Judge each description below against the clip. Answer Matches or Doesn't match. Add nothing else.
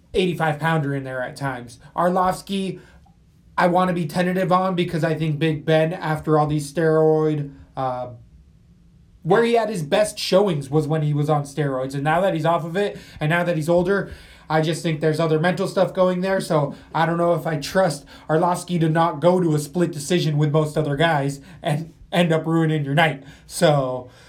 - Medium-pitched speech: Matches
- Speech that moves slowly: Doesn't match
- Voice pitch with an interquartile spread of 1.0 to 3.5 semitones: Matches